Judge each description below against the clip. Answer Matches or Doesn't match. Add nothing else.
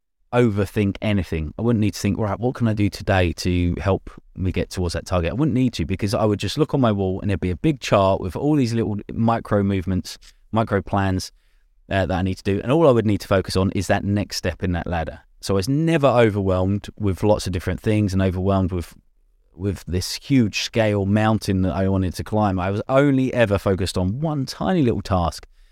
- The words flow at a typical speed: Doesn't match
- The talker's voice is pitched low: Matches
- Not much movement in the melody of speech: Doesn't match